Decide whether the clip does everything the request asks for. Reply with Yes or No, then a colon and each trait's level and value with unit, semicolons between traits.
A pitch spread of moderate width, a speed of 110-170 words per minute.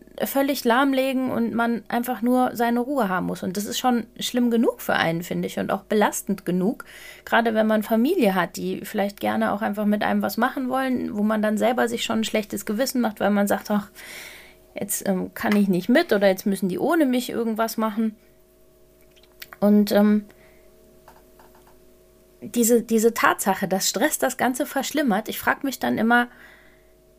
No: average, 3.4 semitones; average, 180 wpm